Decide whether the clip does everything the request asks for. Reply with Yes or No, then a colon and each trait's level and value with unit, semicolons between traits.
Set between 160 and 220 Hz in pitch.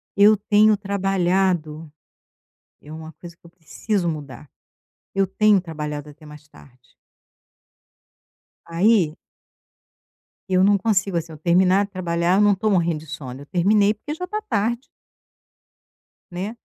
Yes: medium, 185 Hz